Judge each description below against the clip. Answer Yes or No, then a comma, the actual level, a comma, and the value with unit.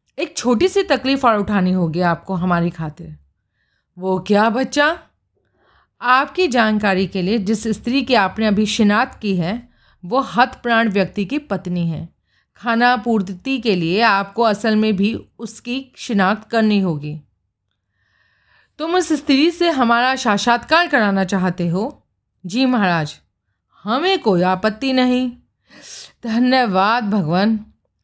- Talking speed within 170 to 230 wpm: No, average, 135 wpm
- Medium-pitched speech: No, high, 215 Hz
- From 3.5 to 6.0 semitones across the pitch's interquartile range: Yes, average, 5.1 semitones